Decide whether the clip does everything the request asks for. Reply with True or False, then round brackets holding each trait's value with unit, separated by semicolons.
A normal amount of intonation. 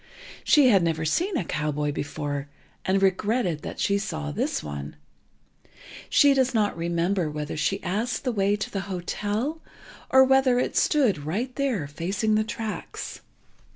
False (7.5 semitones)